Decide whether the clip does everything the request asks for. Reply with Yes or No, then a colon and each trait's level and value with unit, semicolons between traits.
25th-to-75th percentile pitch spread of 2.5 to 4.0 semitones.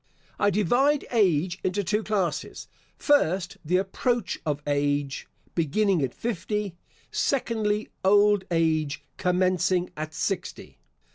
No: average, 4.5 semitones